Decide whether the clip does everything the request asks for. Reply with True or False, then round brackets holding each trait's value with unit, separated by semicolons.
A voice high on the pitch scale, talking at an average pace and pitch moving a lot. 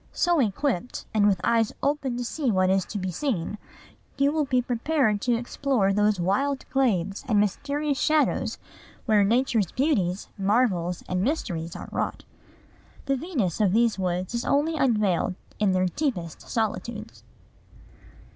True (225 Hz; 145 wpm; 6.0 semitones)